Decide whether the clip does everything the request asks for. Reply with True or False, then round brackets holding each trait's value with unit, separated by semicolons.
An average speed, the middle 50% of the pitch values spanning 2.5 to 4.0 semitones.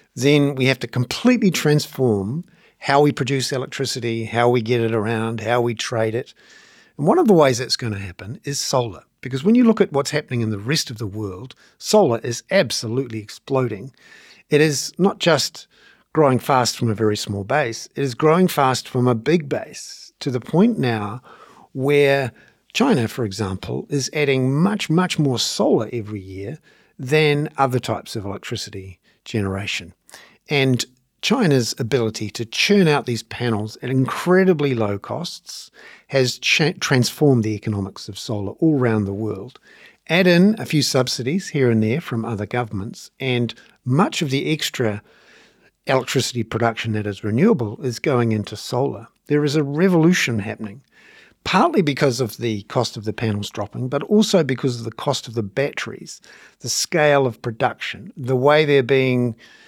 False (170 wpm; 4.5 semitones)